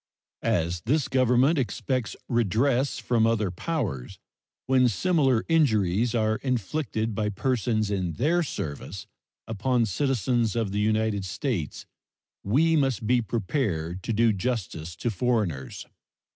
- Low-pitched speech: Yes, low, 115 Hz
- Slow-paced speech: Yes, slow, 120 wpm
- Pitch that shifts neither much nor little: Yes, average, 4.4 semitones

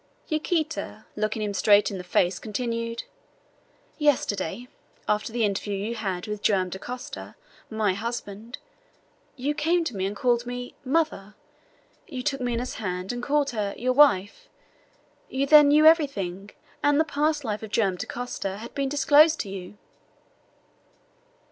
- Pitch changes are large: Yes, wide, 5.8 semitones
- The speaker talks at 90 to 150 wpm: Yes, average, 145 wpm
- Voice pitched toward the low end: No, high, 235 Hz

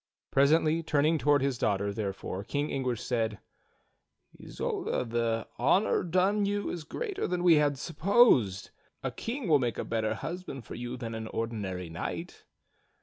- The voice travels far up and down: Yes, wide, 6.8 semitones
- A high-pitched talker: No, low, 135 Hz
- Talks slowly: No, average, 155 wpm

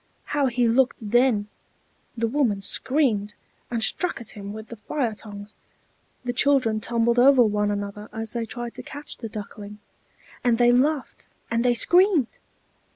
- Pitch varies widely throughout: No, average, 3.2 semitones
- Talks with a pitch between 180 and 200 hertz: No, high, 235 Hz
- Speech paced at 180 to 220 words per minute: No, average, 155 wpm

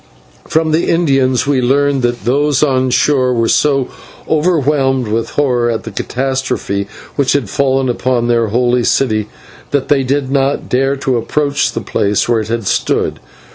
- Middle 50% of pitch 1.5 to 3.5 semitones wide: Yes, average, 2.9 semitones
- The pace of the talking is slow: No, average, 165 wpm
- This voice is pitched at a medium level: No, low, 130 Hz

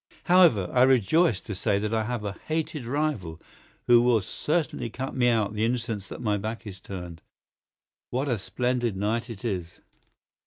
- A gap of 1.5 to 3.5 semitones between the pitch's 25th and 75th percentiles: No, average, 3.9 semitones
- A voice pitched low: Yes, low, 115 Hz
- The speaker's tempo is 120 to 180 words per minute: Yes, average, 170 wpm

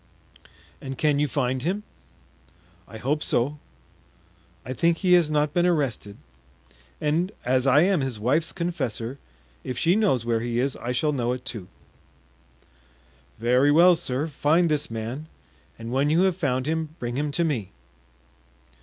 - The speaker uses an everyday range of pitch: Yes, average, 4.6 semitones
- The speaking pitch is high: No, medium, 140 Hz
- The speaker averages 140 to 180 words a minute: Yes, average, 155 wpm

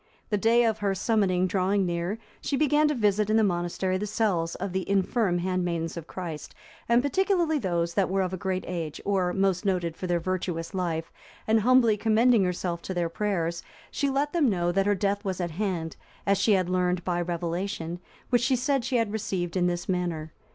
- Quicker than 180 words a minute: Yes, fast, 205 wpm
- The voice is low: No, high, 190 Hz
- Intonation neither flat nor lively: Yes, average, 3.7 semitones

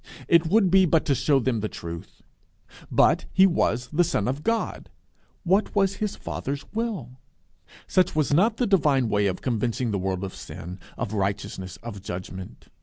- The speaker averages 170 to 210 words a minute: Yes, average, 175 wpm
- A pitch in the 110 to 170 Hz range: Yes, low, 135 Hz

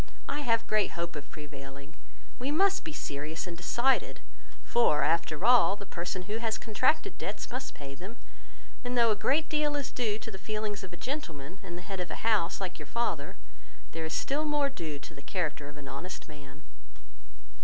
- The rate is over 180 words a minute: Yes, average, 195 wpm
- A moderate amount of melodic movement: No, wide, 7.6 semitones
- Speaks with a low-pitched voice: No, high, 190 Hz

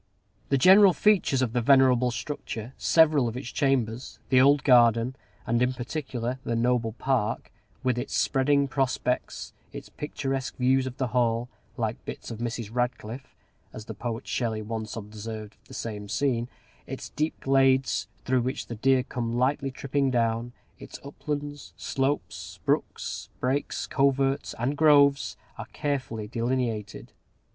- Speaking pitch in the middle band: No, low, 125 Hz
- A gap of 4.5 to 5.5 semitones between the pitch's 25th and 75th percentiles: No, average, 2.9 semitones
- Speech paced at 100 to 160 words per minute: Yes, average, 145 wpm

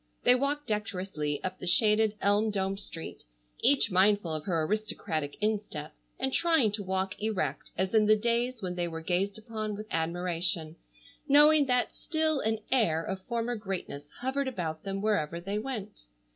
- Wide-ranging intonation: No, average, 4.3 semitones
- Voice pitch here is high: Yes, high, 205 Hz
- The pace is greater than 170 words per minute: No, average, 165 wpm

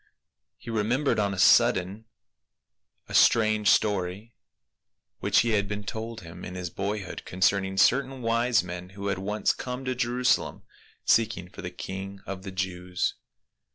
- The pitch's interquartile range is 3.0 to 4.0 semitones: Yes, average, 3.5 semitones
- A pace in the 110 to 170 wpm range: Yes, average, 145 wpm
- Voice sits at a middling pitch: No, low, 100 Hz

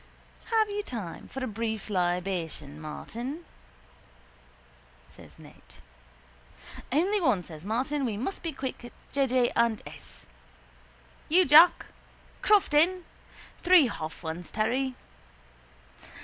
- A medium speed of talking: No, slow, 105 wpm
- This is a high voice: Yes, high, 245 Hz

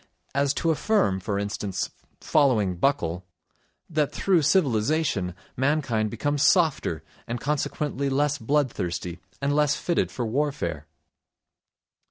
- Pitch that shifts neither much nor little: No, wide, 6.5 semitones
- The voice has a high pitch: No, low, 135 Hz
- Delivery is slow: Yes, slow, 110 wpm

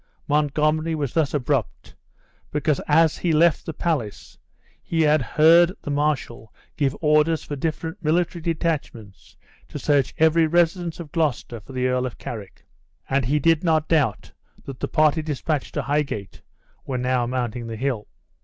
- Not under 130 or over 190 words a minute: Yes, average, 155 wpm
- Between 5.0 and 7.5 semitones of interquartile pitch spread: No, average, 3.9 semitones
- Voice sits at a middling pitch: Yes, medium, 150 Hz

